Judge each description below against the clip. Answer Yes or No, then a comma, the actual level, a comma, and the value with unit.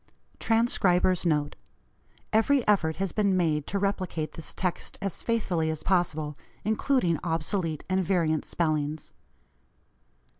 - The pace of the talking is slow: Yes, slow, 115 wpm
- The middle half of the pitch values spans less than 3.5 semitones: No, average, 3.9 semitones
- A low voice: No, medium, 175 Hz